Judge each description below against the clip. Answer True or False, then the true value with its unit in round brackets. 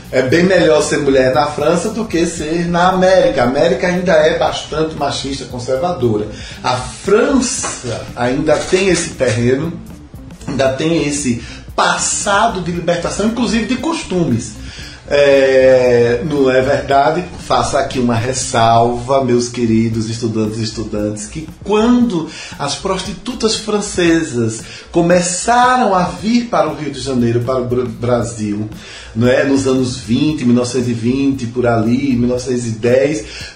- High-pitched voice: False (135 Hz)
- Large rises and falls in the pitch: True (6.4 semitones)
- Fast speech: False (130 wpm)